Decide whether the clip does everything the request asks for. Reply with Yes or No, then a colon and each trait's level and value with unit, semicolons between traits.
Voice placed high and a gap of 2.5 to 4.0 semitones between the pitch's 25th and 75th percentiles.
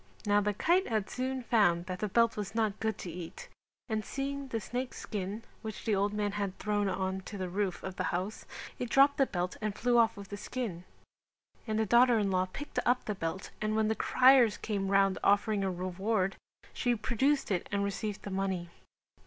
Yes: high, 210 Hz; average, 3.3 semitones